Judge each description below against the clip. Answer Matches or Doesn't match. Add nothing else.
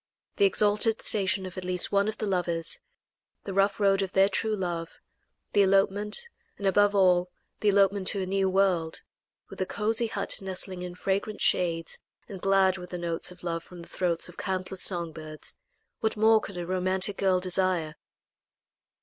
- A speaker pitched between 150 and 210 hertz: Matches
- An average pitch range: Doesn't match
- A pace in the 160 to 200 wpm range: Matches